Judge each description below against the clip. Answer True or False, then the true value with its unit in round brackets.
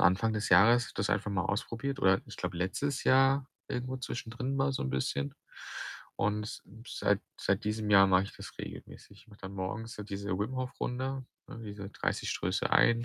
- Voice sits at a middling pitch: False (105 Hz)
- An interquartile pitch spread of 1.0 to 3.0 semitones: False (4.5 semitones)